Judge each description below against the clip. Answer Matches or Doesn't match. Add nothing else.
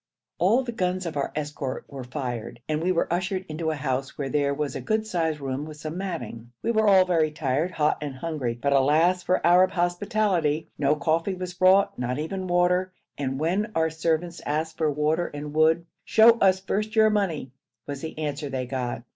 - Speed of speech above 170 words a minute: Matches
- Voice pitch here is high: Doesn't match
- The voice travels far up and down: Doesn't match